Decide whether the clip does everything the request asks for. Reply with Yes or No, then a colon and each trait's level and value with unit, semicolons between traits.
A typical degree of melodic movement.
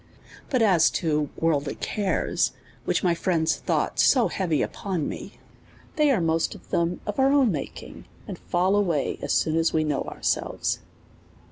Yes: average, 4.4 semitones